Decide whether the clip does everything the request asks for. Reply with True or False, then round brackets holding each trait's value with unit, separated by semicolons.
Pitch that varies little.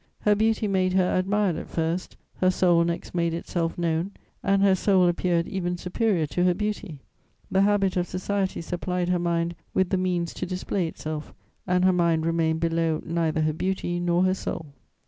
True (2.0 semitones)